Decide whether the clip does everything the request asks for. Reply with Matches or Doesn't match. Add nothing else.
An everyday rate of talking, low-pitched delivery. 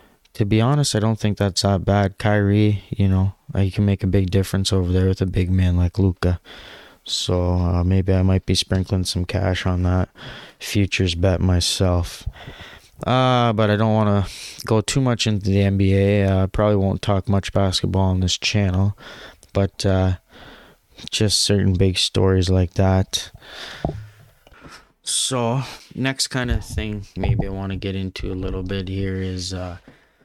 Matches